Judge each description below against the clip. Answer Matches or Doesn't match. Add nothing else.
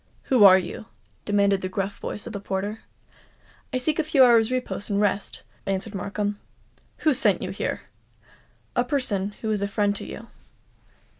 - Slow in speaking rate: Doesn't match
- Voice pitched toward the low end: Doesn't match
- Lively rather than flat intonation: Doesn't match